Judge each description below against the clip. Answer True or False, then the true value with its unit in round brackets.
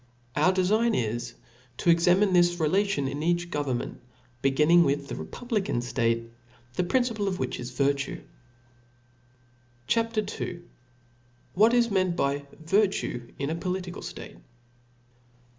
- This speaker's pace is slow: True (115 wpm)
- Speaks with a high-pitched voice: False (175 Hz)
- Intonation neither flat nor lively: False (6.0 semitones)